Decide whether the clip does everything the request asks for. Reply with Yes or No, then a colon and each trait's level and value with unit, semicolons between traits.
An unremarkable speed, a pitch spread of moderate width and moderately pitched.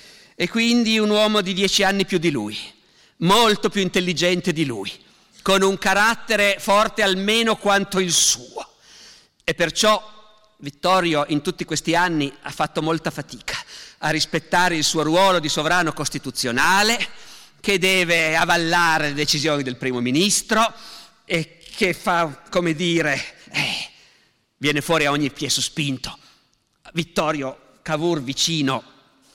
Yes: average, 135 wpm; average, 4.7 semitones; medium, 170 Hz